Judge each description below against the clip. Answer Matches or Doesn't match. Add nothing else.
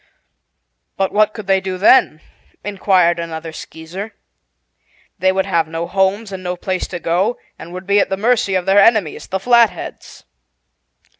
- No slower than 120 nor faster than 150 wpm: Doesn't match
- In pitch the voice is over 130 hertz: Matches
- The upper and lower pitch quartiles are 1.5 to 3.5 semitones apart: Matches